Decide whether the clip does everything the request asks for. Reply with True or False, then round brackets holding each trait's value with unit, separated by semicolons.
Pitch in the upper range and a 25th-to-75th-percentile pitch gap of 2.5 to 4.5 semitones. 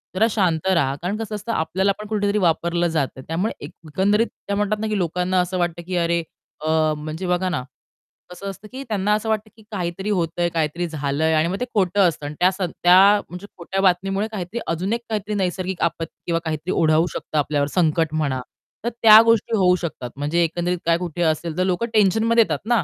False (180 Hz; 3.8 semitones)